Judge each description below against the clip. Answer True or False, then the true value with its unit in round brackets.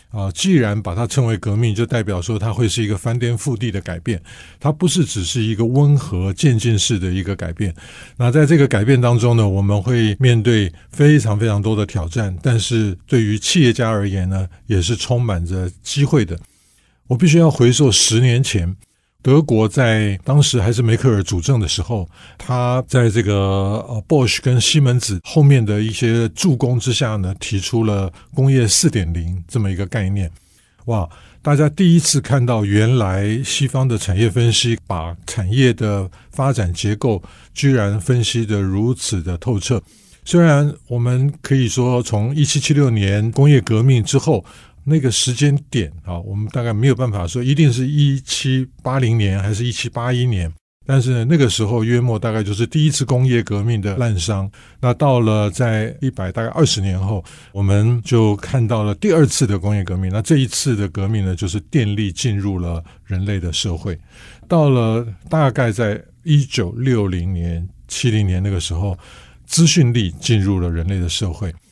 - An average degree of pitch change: True (4.4 semitones)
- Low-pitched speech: True (115 Hz)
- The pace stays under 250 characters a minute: False (265 characters per minute)